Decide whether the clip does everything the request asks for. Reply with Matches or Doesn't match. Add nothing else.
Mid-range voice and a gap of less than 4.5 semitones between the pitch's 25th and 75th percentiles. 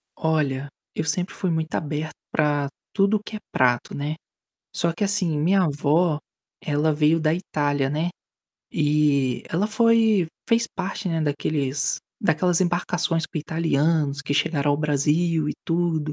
Matches